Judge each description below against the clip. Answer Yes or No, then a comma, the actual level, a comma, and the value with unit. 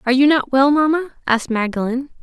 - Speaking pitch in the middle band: No, very high, 265 Hz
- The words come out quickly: No, average, 190 wpm